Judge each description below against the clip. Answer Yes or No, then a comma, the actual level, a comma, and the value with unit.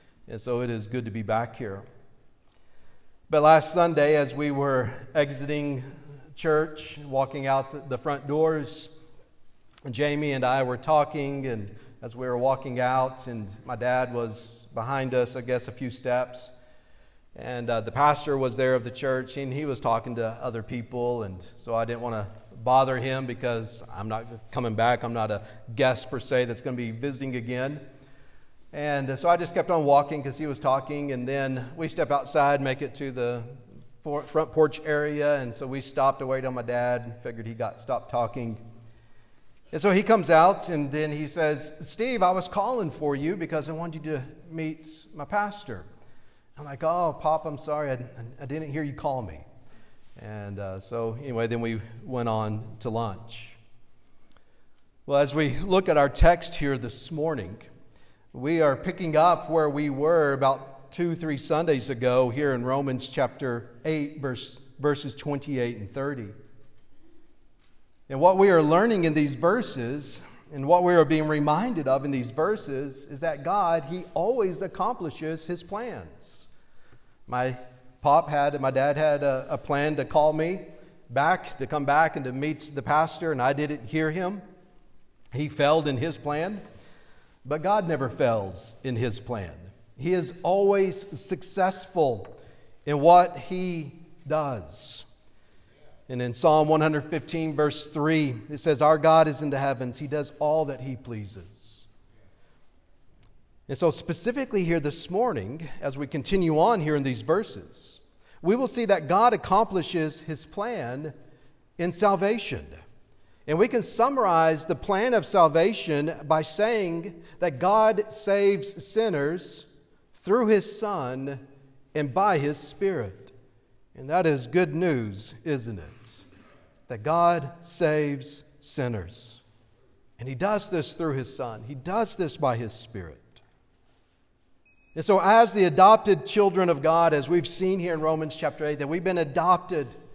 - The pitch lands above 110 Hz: Yes, medium, 140 Hz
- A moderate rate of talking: Yes, average, 165 wpm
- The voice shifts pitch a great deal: No, average, 4.5 semitones